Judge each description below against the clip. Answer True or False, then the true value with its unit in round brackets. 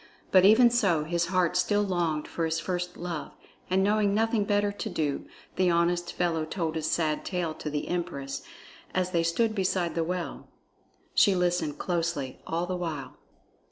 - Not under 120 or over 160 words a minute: False (170 wpm)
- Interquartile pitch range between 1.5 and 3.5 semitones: True (2.6 semitones)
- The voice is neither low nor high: True (175 Hz)